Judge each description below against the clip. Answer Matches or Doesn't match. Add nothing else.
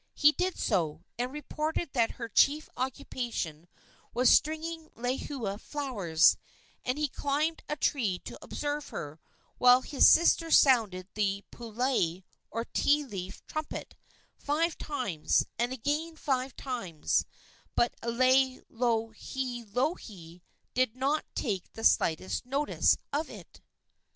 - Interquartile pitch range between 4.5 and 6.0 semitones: Matches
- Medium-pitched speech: Doesn't match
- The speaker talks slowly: Matches